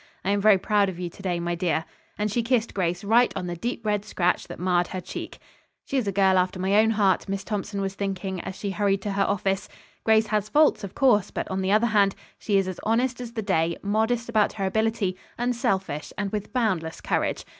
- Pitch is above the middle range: Yes, high, 200 Hz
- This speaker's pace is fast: Yes, fast, 230 wpm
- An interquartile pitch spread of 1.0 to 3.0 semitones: Yes, average, 2.7 semitones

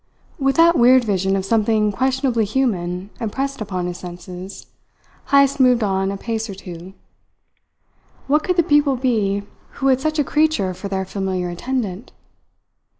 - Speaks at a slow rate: No, average, 150 wpm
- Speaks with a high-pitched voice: Yes, high, 215 Hz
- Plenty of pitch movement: Yes, wide, 5.8 semitones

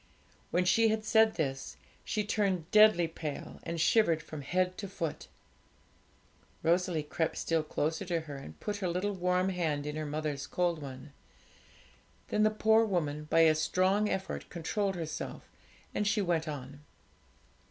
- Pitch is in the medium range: Yes, medium, 170 Hz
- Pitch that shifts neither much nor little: Yes, average, 4.4 semitones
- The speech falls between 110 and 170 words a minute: Yes, average, 155 wpm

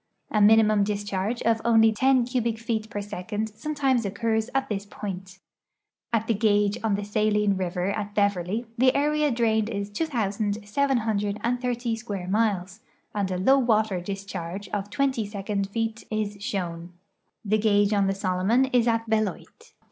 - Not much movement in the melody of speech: Yes, narrow, 2.3 semitones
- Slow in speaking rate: No, average, 150 wpm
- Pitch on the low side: No, high, 215 Hz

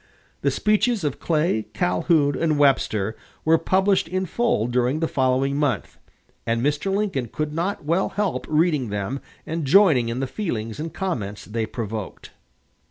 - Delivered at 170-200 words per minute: No, average, 155 wpm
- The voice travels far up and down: Yes, wide, 6.5 semitones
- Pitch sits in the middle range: Yes, medium, 145 Hz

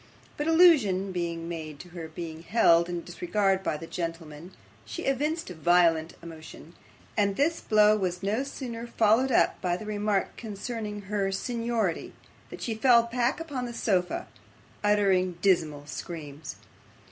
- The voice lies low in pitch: No, high, 195 Hz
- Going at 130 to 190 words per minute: Yes, average, 145 wpm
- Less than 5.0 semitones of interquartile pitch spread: No, average, 5.3 semitones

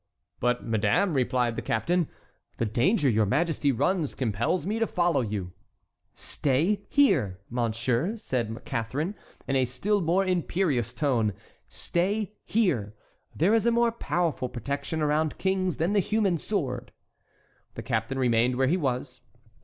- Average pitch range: No, wide, 7.4 semitones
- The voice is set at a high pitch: No, medium, 140 Hz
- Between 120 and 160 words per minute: Yes, average, 140 wpm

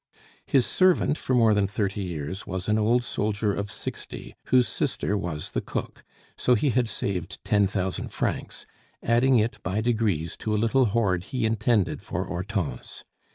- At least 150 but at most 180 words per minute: Yes, average, 165 wpm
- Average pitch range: Yes, average, 3.4 semitones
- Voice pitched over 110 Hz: No, low, 105 Hz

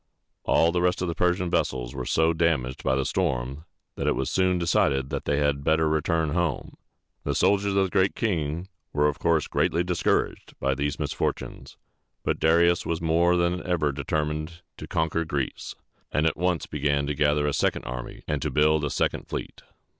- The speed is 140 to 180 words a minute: No, average, 190 wpm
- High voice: No, very low, 80 Hz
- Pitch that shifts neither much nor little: Yes, average, 3.1 semitones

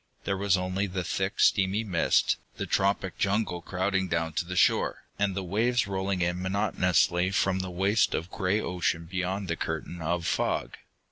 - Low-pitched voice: Yes, very low, 95 Hz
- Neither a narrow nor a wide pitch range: No, narrow, 1.9 semitones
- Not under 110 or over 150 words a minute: No, average, 175 wpm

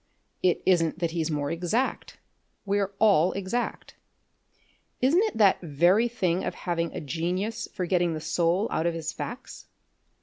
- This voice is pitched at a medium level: Yes, medium, 180 Hz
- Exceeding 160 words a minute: No, average, 155 wpm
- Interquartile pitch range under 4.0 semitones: Yes, average, 3.6 semitones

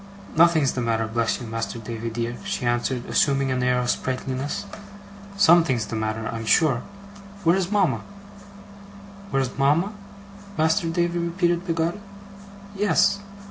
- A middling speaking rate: No, slow, 130 wpm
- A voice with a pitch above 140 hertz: No, low, 135 Hz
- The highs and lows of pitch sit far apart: Yes, wide, 6.3 semitones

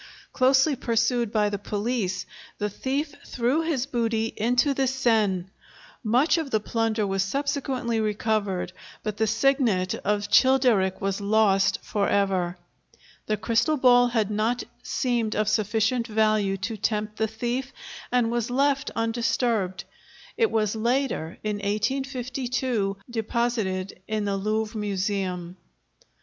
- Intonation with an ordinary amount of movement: Yes, average, 3.4 semitones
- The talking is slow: Yes, slow, 130 wpm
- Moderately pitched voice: No, high, 220 Hz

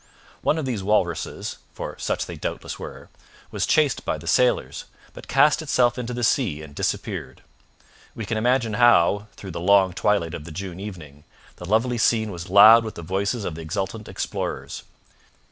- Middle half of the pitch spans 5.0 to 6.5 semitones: Yes, wide, 5.6 semitones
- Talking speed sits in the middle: Yes, average, 180 wpm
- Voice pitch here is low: Yes, low, 105 Hz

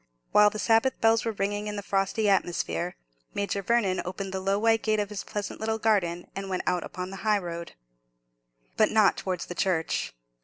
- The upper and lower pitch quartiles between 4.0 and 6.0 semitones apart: No, narrow, 2.6 semitones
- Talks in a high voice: Yes, high, 200 Hz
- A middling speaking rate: Yes, average, 195 wpm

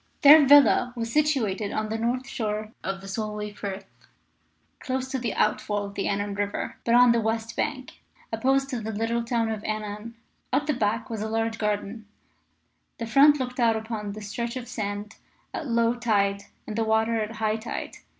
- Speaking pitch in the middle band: No, high, 225 Hz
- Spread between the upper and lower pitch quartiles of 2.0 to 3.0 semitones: Yes, narrow, 2.5 semitones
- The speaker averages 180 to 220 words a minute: Yes, average, 190 wpm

